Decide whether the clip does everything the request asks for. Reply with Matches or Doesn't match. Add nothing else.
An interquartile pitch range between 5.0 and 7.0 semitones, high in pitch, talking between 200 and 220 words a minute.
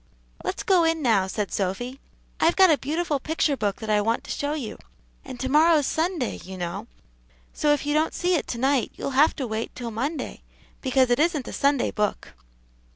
Matches